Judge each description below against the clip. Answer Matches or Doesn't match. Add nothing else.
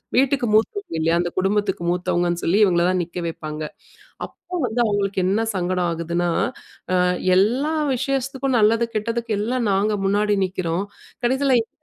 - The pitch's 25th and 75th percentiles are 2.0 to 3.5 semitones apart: Doesn't match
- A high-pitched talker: Matches